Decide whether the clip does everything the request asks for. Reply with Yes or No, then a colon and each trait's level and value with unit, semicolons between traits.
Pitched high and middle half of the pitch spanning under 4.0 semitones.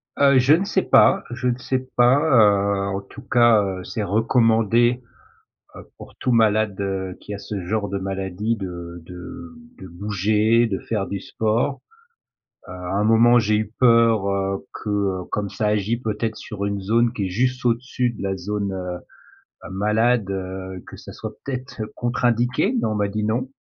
No: low, 110 Hz; average, 3.5 semitones